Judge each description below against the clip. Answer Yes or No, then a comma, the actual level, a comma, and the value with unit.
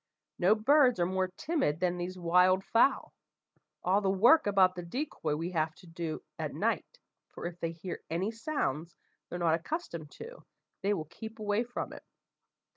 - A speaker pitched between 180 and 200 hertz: Yes, medium, 185 Hz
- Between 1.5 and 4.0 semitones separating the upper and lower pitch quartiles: No, average, 4.5 semitones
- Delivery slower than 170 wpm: No, average, 175 wpm